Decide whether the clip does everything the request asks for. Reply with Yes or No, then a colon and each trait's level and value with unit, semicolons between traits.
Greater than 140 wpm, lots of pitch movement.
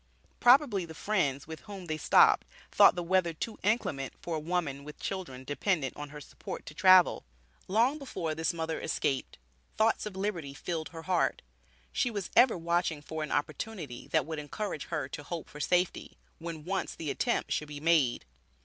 No: average, 180 wpm; average, 4.1 semitones